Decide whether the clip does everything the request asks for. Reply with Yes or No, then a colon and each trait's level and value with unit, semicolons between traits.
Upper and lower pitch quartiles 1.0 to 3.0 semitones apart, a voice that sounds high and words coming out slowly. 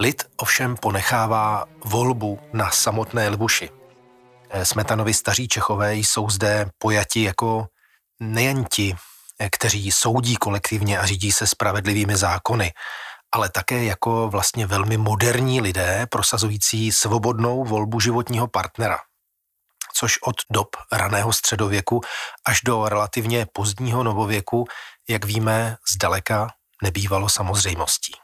No: narrow, 2.4 semitones; low, 110 Hz; slow, 110 wpm